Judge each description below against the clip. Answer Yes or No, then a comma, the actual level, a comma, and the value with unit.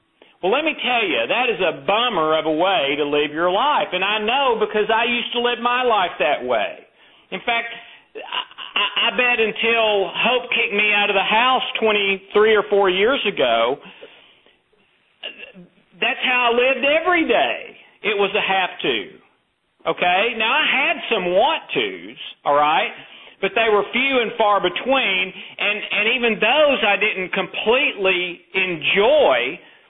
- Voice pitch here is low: No, high, 215 Hz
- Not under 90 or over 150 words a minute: No, average, 165 wpm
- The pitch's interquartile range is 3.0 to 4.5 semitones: Yes, average, 3.9 semitones